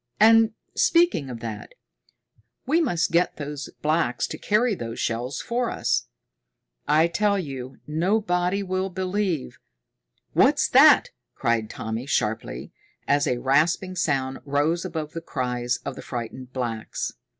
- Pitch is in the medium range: Yes, medium, 150 Hz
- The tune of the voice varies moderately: No, wide, 7.0 semitones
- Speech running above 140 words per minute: No, slow, 135 wpm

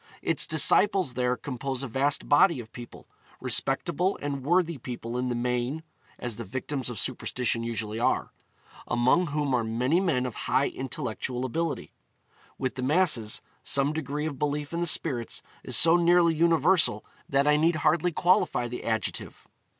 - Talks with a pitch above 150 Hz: No, medium, 140 Hz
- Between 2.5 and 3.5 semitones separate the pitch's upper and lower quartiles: No, average, 4.6 semitones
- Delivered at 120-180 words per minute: Yes, average, 160 wpm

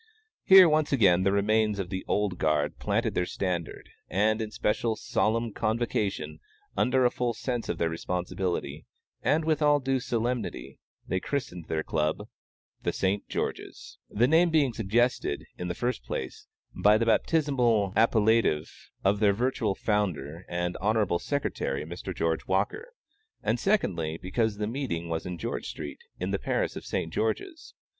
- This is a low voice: Yes, low, 105 Hz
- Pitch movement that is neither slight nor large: No, wide, 5.7 semitones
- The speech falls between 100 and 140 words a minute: No, average, 155 wpm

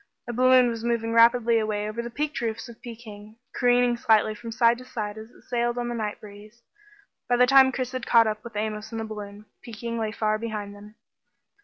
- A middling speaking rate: No, fast, 220 wpm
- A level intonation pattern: Yes, narrow, 2.0 semitones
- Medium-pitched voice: No, high, 230 Hz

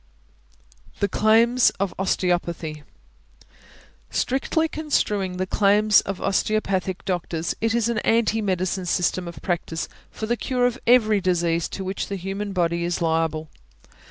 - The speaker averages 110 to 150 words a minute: Yes, slow, 135 wpm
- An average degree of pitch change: Yes, average, 3.8 semitones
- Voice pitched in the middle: No, high, 195 Hz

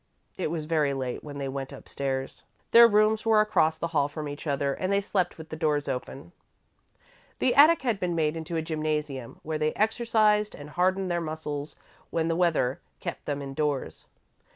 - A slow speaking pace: No, average, 190 wpm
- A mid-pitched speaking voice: Yes, medium, 160 Hz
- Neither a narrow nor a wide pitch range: Yes, average, 4.6 semitones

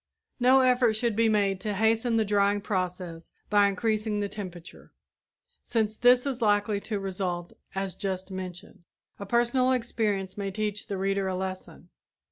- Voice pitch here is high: Yes, high, 205 Hz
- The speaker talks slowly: No, average, 155 wpm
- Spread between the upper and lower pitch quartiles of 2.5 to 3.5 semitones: Yes, average, 2.9 semitones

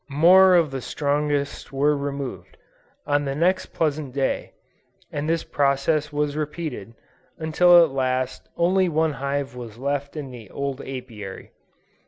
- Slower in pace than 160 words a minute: Yes, average, 140 wpm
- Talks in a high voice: No, medium, 145 Hz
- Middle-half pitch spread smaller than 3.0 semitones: Yes, narrow, 2.5 semitones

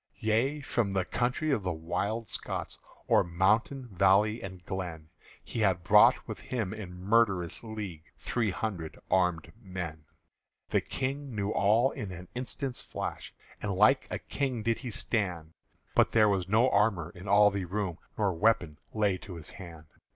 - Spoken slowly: No, average, 165 wpm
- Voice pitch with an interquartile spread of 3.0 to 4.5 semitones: Yes, average, 4.0 semitones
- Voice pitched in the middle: No, low, 100 Hz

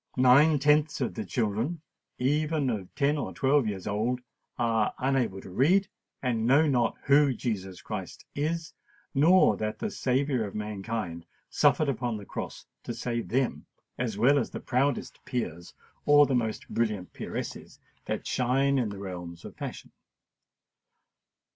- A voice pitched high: No, low, 125 Hz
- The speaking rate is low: No, average, 150 wpm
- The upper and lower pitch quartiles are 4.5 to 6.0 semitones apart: Yes, average, 4.8 semitones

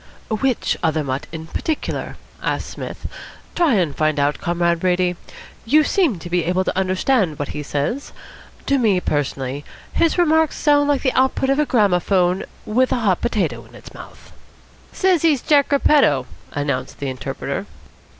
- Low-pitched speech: No, medium, 185 Hz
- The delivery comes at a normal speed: Yes, average, 160 wpm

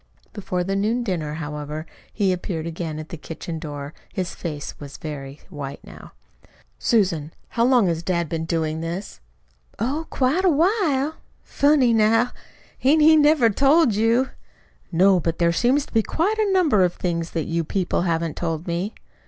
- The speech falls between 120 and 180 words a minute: Yes, average, 170 wpm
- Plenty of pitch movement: Yes, wide, 7.3 semitones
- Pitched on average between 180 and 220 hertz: Yes, medium, 185 Hz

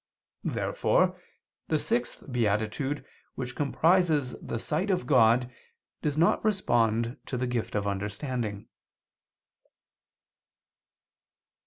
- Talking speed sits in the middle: No, slow, 95 wpm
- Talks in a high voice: No, low, 125 Hz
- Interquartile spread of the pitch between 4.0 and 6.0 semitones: Yes, average, 5.3 semitones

